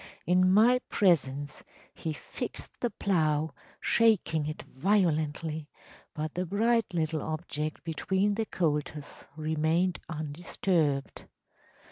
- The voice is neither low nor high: Yes, medium, 160 Hz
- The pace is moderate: No, slow, 100 wpm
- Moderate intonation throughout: Yes, average, 3.8 semitones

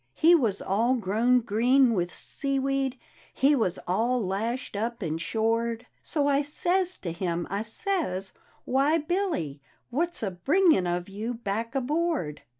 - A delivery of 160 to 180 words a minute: No, average, 150 wpm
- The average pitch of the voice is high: Yes, high, 235 Hz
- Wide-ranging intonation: Yes, wide, 6.3 semitones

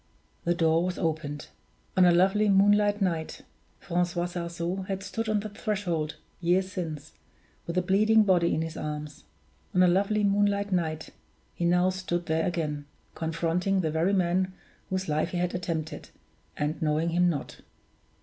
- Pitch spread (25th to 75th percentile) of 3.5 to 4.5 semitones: No, average, 2.8 semitones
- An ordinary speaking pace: Yes, average, 160 wpm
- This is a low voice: No, medium, 175 Hz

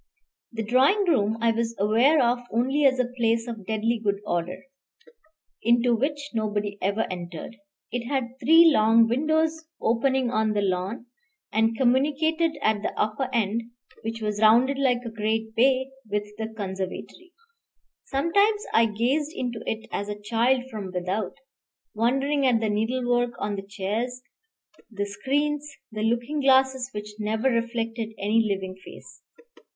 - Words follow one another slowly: No, average, 145 wpm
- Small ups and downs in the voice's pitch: No, average, 3.7 semitones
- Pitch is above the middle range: Yes, high, 230 Hz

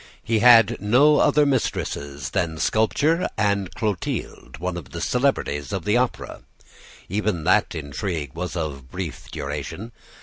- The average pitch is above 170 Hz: No, very low, 95 Hz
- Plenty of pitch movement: Yes, wide, 7.1 semitones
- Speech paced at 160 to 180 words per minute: No, slow, 135 wpm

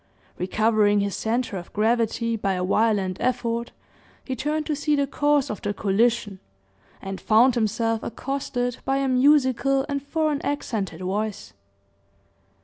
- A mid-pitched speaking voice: No, high, 230 Hz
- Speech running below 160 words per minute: Yes, average, 140 wpm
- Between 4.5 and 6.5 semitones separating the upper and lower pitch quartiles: Yes, average, 4.8 semitones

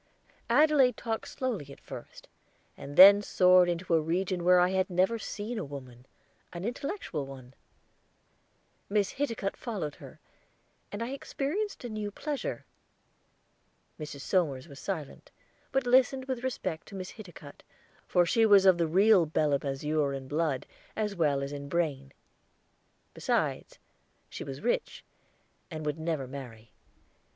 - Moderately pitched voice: Yes, medium, 180 Hz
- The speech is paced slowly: No, average, 145 wpm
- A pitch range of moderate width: No, wide, 7.2 semitones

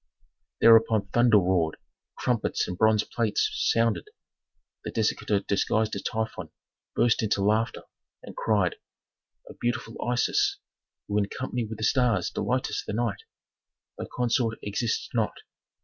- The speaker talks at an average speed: No, slow, 130 wpm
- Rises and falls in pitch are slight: Yes, narrow, 2.3 semitones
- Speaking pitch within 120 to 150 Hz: No, low, 110 Hz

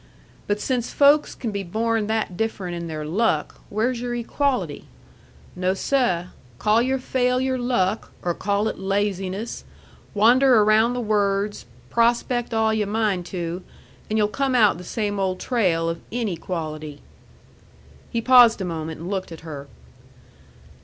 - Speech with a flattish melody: No, average, 4.5 semitones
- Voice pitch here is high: Yes, high, 210 Hz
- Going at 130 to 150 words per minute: Yes, average, 145 wpm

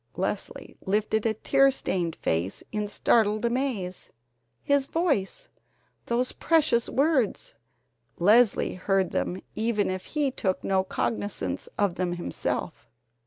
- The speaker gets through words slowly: Yes, slow, 120 wpm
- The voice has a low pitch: No, high, 210 Hz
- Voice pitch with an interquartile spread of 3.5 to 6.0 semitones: Yes, wide, 5.5 semitones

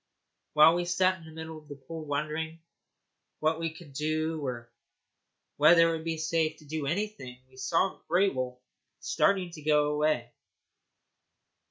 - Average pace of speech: Yes, average, 160 wpm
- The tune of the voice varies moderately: No, narrow, 2.1 semitones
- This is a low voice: No, medium, 155 Hz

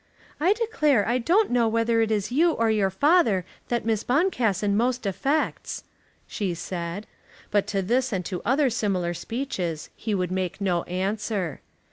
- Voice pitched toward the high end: Yes, high, 220 Hz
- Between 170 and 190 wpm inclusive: No, average, 160 wpm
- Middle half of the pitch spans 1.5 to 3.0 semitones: No, average, 5.1 semitones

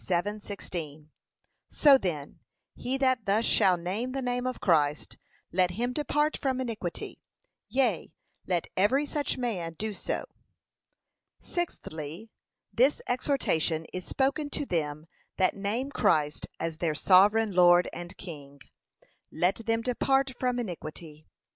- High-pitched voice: Yes, high, 200 Hz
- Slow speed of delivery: Yes, slow, 125 wpm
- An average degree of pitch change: No, wide, 7.0 semitones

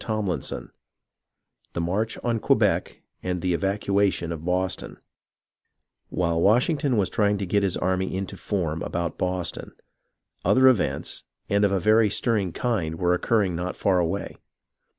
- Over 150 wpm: No, average, 145 wpm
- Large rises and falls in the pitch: No, average, 3.0 semitones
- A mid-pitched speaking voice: No, very low, 95 Hz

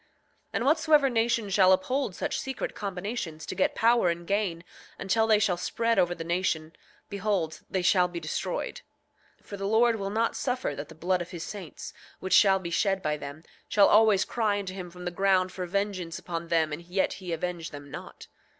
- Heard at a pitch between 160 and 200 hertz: Yes, high, 190 Hz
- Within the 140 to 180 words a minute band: No, average, 200 wpm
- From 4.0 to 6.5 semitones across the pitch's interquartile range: No, average, 3.6 semitones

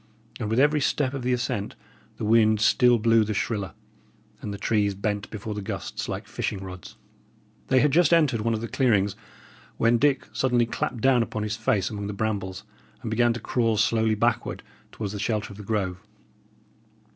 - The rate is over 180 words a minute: Yes, average, 190 wpm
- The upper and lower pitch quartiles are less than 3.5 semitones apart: Yes, average, 2.8 semitones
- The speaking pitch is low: Yes, low, 110 Hz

